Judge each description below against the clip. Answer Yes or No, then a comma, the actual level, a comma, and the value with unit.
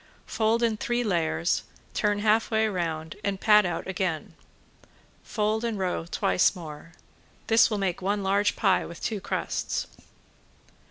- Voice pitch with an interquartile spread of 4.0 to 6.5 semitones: No, average, 3.6 semitones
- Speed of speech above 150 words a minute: No, average, 145 wpm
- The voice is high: Yes, high, 200 Hz